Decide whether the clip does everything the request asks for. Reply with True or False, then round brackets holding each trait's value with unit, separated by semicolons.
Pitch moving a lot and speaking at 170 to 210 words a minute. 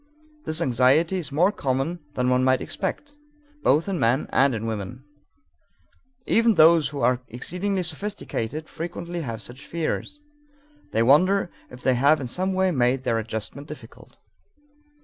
False (5.7 semitones; 150 wpm)